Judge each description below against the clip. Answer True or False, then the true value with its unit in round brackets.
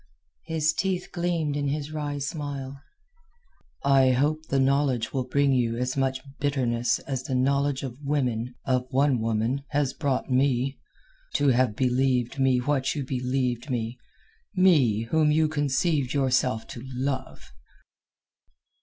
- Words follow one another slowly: True (125 wpm)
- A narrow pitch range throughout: True (2.3 semitones)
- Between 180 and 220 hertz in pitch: False (135 Hz)